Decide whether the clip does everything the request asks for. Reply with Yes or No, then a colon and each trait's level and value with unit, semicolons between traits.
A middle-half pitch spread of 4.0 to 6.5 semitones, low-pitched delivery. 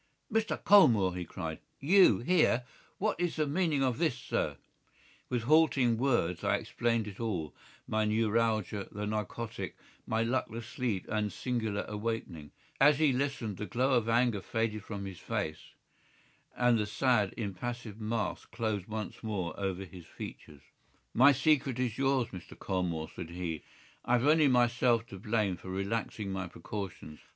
Yes: average, 4.3 semitones; low, 115 Hz